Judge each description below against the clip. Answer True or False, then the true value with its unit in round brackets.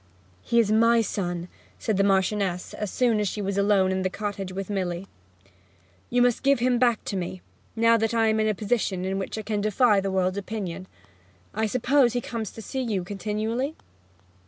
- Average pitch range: True (3.2 semitones)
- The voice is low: False (210 Hz)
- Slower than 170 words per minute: False (200 wpm)